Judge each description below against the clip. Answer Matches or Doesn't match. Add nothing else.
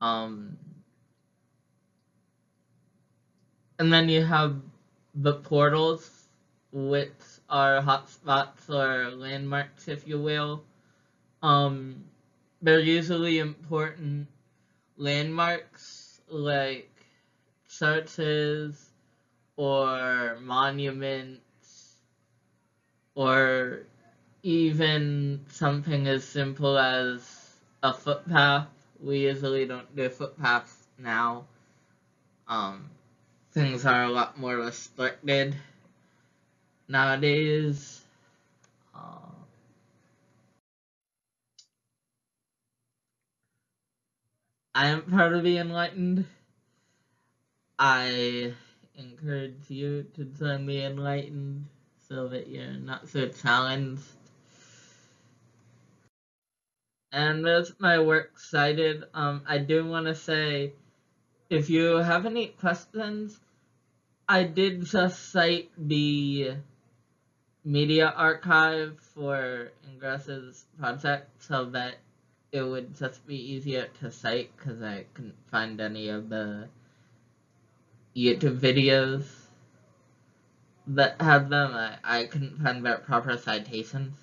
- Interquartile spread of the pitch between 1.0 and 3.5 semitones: Matches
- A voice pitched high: Doesn't match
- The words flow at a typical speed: Doesn't match